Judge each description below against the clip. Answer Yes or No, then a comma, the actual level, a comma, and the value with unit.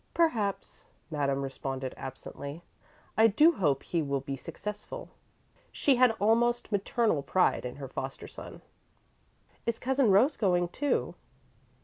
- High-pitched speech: Yes, high, 195 Hz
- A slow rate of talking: Yes, slow, 125 wpm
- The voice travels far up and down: Yes, wide, 9.0 semitones